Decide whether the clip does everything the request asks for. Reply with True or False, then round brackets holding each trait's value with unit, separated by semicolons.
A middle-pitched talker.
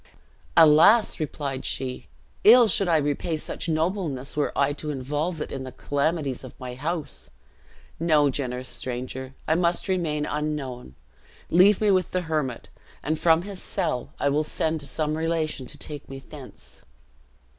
True (150 Hz)